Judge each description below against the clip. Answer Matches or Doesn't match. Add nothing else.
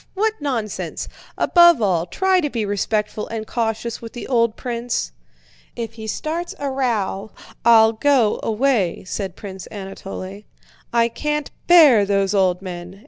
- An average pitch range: Matches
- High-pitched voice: Matches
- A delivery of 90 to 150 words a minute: Matches